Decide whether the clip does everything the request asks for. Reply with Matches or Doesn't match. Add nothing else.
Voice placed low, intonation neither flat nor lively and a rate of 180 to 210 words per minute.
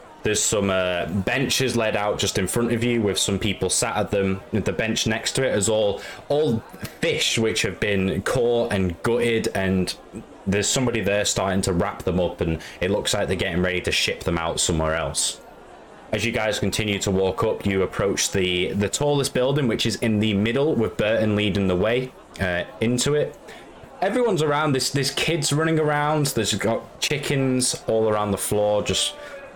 Matches